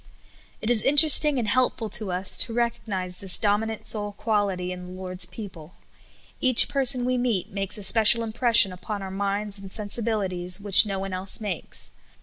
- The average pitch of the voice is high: Yes, high, 205 Hz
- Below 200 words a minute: Yes, average, 175 wpm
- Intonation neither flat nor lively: Yes, average, 3.5 semitones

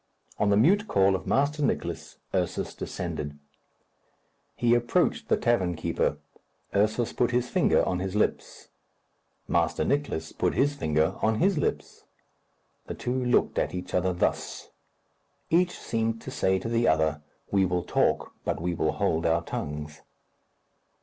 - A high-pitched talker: No, low, 100 Hz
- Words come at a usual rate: Yes, average, 150 wpm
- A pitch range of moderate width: No, wide, 6.1 semitones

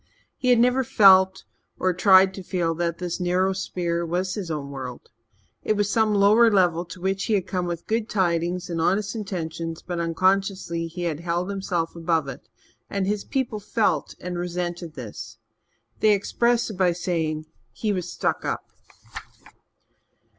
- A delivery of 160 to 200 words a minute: Yes, average, 165 wpm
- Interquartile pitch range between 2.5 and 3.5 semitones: Yes, average, 2.9 semitones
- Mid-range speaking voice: Yes, medium, 180 Hz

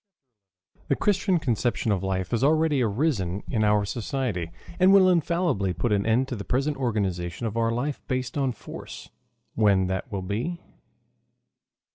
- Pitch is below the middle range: Yes, low, 120 Hz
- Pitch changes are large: Yes, wide, 6.0 semitones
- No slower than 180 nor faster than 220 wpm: No, average, 155 wpm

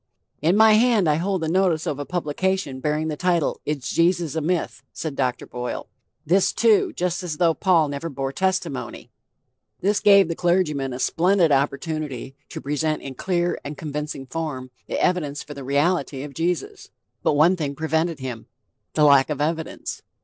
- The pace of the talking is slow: No, average, 175 wpm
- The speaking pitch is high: No, medium, 160 Hz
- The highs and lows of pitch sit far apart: No, average, 4.0 semitones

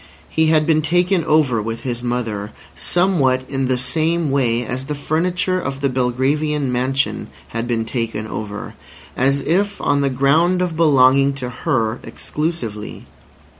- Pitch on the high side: No, low, 135 Hz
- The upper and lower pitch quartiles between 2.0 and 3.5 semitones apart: No, average, 4.2 semitones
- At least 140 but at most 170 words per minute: Yes, average, 150 wpm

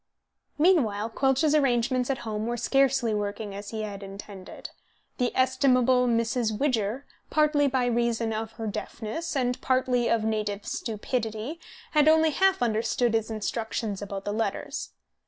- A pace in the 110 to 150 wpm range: Yes, average, 140 wpm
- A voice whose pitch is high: Yes, high, 235 Hz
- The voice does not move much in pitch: No, average, 3.4 semitones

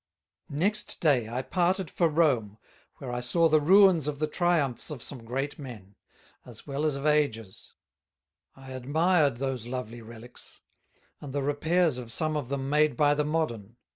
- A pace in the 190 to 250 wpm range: No, average, 170 wpm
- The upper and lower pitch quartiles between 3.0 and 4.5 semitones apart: Yes, average, 4.1 semitones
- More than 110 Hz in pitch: Yes, medium, 140 Hz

